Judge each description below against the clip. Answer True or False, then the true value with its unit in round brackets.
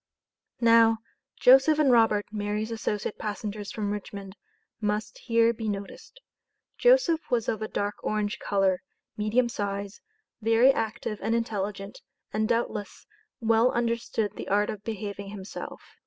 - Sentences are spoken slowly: True (130 wpm)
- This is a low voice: False (215 Hz)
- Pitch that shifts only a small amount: True (2.1 semitones)